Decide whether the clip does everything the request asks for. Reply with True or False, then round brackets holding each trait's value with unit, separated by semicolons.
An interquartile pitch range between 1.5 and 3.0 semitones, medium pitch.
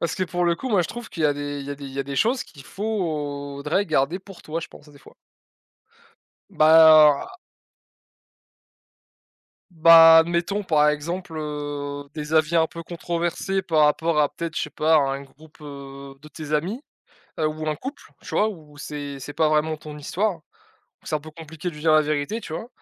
True (2.6 semitones; 155 Hz)